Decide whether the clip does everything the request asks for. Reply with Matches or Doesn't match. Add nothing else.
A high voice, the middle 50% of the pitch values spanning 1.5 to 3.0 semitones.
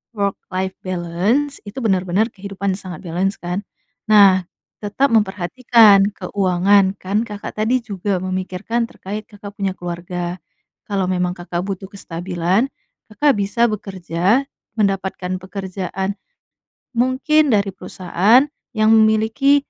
Matches